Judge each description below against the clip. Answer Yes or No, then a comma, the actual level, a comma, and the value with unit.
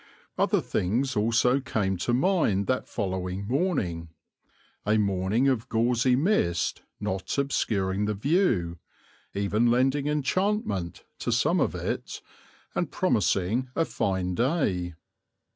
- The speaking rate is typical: No, slow, 115 wpm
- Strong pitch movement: Yes, wide, 6.0 semitones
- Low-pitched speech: Yes, low, 110 Hz